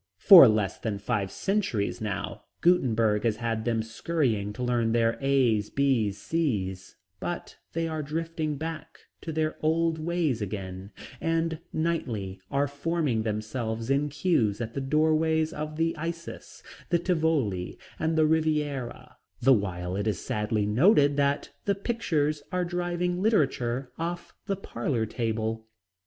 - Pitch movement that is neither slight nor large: No, wide, 6.7 semitones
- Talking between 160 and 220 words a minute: No, average, 140 wpm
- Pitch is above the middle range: No, medium, 140 Hz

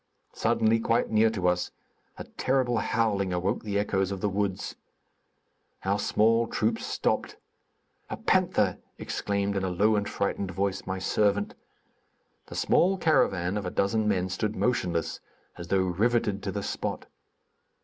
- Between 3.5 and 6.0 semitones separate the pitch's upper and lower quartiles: No, average, 2.8 semitones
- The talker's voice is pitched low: Yes, low, 100 Hz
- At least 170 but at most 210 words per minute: No, average, 150 wpm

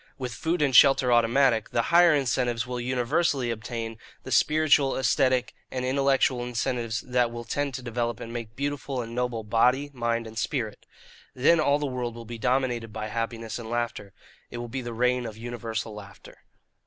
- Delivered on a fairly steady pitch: Yes, narrow, 2.3 semitones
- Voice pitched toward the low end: Yes, low, 120 Hz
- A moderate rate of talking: Yes, average, 180 wpm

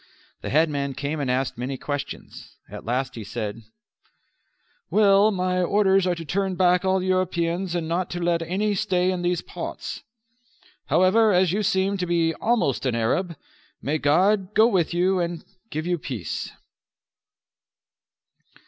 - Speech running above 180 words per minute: No, average, 150 wpm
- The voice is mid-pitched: Yes, medium, 175 Hz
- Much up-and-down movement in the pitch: No, average, 4.1 semitones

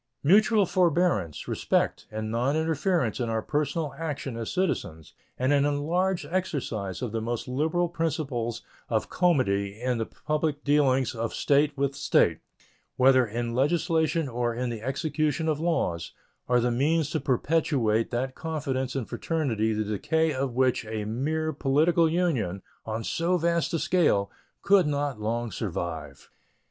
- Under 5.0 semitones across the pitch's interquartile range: No, wide, 5.6 semitones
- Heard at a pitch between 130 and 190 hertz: Yes, low, 135 Hz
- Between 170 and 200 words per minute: No, average, 145 wpm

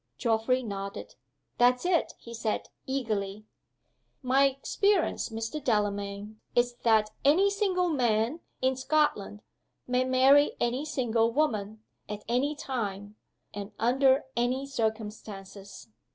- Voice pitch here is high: Yes, high, 240 Hz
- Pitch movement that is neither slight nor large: Yes, average, 4.2 semitones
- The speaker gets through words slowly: Yes, slow, 110 wpm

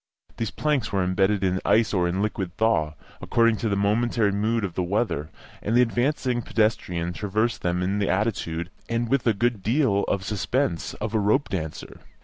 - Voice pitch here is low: Yes, low, 105 Hz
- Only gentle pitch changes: No, average, 3.8 semitones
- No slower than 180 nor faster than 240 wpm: Yes, average, 190 wpm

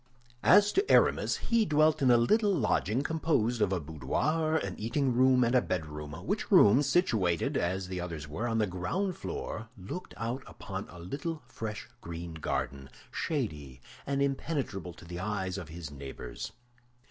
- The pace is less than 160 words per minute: No, average, 165 wpm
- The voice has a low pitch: Yes, low, 110 Hz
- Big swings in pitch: Yes, wide, 8.4 semitones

